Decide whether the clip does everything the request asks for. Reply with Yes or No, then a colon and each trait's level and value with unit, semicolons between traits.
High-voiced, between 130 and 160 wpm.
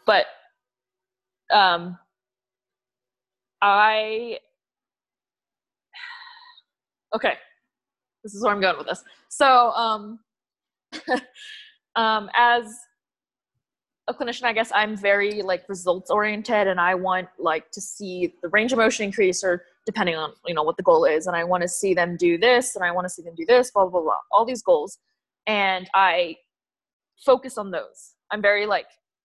Yes: high, 205 Hz; average, 155 wpm